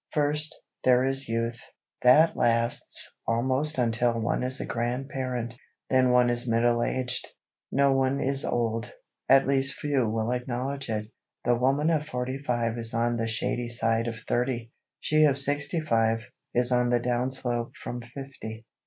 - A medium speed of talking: Yes, average, 155 wpm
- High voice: No, low, 125 Hz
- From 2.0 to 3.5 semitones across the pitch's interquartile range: Yes, narrow, 2.4 semitones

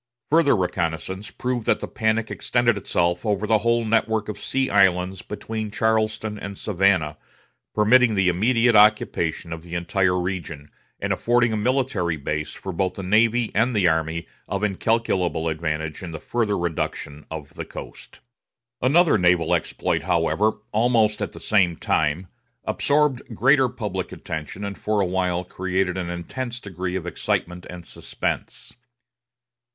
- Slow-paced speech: No, average, 150 wpm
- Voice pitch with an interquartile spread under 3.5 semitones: No, average, 4.3 semitones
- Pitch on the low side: Yes, low, 100 Hz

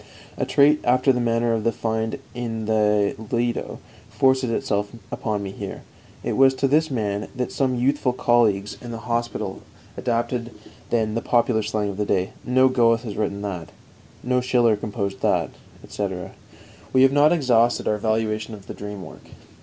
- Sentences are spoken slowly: No, average, 170 wpm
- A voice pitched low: Yes, low, 115 Hz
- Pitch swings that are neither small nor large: Yes, average, 3.1 semitones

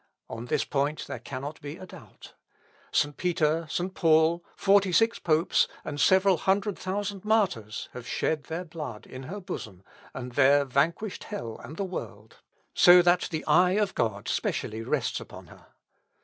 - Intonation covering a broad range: Yes, wide, 5.8 semitones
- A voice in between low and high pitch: Yes, medium, 160 Hz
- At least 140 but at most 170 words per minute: Yes, average, 165 wpm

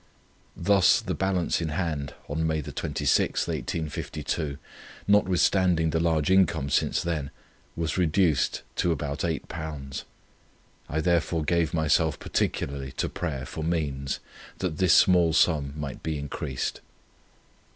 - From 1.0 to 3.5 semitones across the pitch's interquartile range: Yes, average, 3.0 semitones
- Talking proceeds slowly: Yes, slow, 120 wpm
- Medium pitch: No, very low, 80 Hz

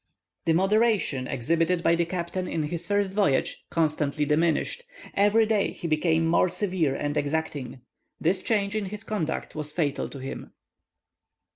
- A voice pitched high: No, medium, 170 Hz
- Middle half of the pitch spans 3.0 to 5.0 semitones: Yes, average, 4.7 semitones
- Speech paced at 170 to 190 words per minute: No, average, 150 wpm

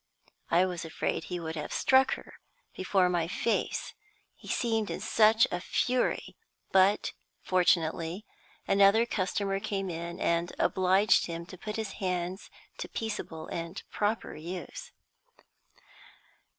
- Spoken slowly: Yes, slow, 125 wpm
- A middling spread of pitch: Yes, average, 3.6 semitones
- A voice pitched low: No, medium, 185 Hz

